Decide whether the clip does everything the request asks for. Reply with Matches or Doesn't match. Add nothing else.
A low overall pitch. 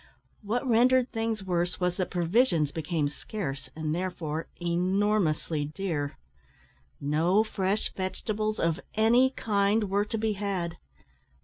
Doesn't match